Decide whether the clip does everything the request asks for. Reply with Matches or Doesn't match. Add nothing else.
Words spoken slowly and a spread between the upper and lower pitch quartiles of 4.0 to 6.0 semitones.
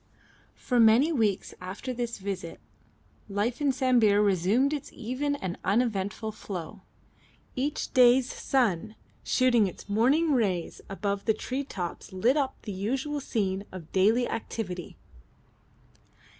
Matches